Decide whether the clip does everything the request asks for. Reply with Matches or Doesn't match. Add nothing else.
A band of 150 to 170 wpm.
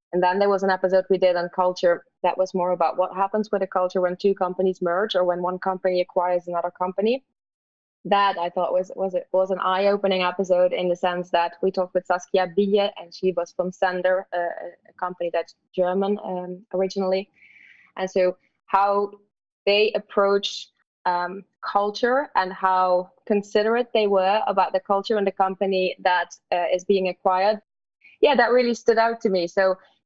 Doesn't match